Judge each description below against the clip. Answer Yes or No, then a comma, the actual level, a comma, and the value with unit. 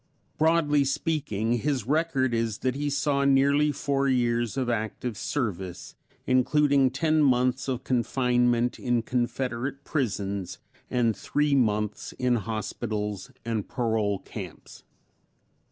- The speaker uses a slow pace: Yes, slow, 115 wpm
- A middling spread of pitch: Yes, average, 3.5 semitones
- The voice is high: No, low, 125 Hz